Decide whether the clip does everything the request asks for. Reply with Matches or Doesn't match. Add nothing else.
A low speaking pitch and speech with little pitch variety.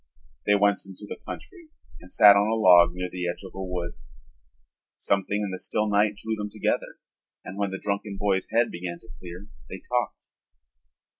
Matches